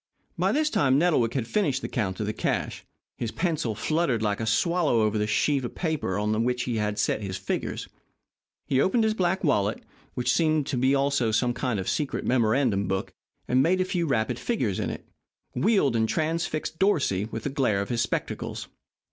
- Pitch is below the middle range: Yes, low, 125 Hz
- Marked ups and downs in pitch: Yes, wide, 6.4 semitones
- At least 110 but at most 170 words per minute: No, average, 195 wpm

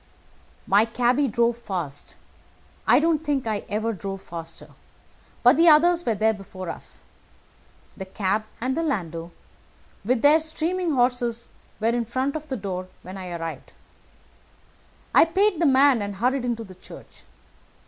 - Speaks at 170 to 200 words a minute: No, average, 150 wpm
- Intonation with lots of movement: Yes, wide, 6.6 semitones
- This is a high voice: Yes, high, 235 Hz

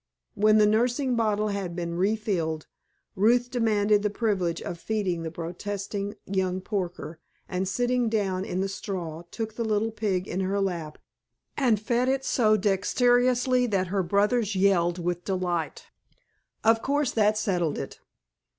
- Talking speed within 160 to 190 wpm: No, average, 150 wpm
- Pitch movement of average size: Yes, average, 3.4 semitones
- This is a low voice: No, high, 205 Hz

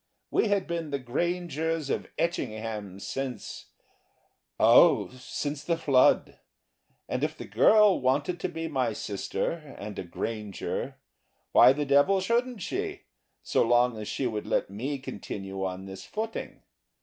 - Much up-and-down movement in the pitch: Yes, wide, 7.7 semitones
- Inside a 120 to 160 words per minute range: Yes, average, 140 wpm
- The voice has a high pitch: No, low, 135 Hz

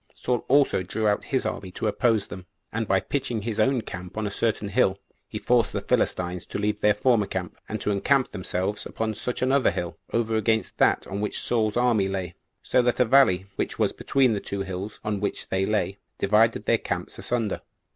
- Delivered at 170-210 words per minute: Yes, fast, 205 wpm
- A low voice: Yes, low, 105 Hz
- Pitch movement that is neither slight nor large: Yes, average, 3.3 semitones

